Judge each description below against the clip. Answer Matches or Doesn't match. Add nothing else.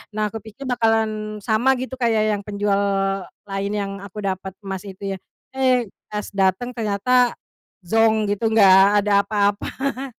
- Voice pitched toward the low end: Doesn't match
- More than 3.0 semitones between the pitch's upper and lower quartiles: Doesn't match